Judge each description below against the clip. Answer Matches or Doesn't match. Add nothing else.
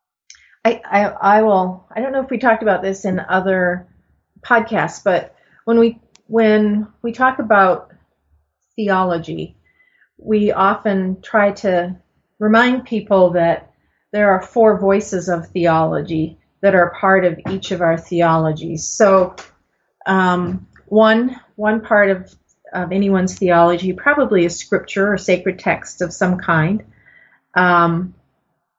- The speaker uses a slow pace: Matches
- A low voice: Doesn't match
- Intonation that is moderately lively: Matches